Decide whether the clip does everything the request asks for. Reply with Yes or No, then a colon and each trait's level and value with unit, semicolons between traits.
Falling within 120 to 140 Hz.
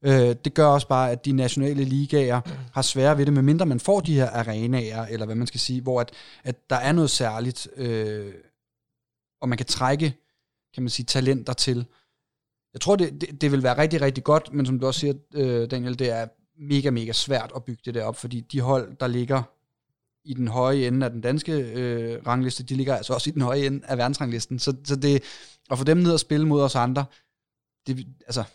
Yes: low, 130 Hz